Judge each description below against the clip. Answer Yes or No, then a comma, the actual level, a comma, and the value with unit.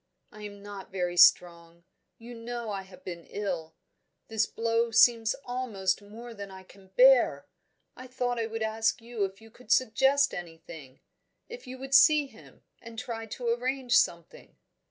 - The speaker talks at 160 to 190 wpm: Yes, average, 165 wpm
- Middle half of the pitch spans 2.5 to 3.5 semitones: No, average, 4.3 semitones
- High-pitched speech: Yes, high, 225 Hz